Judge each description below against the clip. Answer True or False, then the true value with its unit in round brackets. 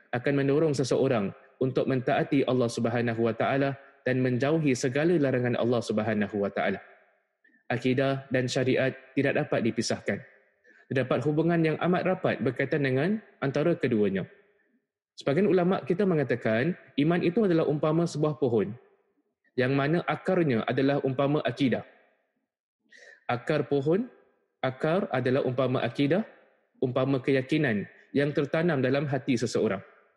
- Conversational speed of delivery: True (120 wpm)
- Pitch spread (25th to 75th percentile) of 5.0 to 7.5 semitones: False (3.4 semitones)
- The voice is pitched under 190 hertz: True (140 Hz)